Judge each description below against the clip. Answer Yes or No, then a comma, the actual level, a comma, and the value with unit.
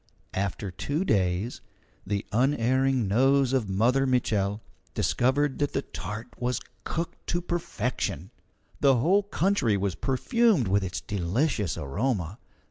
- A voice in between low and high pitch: No, low, 125 Hz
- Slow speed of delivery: Yes, slow, 125 wpm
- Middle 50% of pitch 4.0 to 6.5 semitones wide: Yes, wide, 5.6 semitones